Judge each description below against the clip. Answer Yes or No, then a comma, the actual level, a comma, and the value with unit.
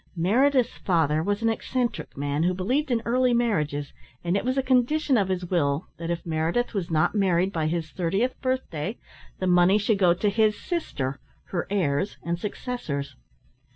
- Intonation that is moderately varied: No, wide, 6.2 semitones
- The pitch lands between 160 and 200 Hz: Yes, high, 190 Hz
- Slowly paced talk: No, average, 175 wpm